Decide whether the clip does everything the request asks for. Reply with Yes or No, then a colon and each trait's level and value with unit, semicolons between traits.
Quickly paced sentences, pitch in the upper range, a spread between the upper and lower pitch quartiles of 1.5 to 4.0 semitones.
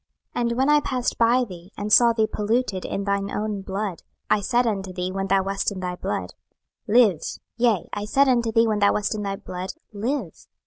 Yes: fast, 215 wpm; high, 210 Hz; average, 3.3 semitones